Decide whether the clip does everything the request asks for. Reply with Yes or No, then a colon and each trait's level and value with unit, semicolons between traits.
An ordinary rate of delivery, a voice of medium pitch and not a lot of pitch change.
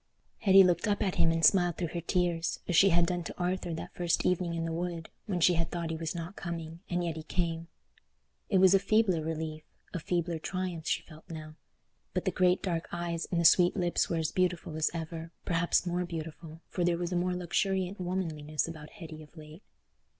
No: fast, 215 wpm; medium, 170 Hz; narrow, 1.8 semitones